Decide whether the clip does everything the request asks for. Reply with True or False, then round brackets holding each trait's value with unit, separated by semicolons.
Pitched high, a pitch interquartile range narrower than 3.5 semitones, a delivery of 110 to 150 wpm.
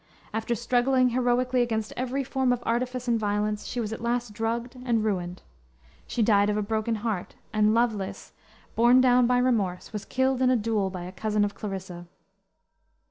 False (230 Hz; 2.9 semitones; 180 wpm)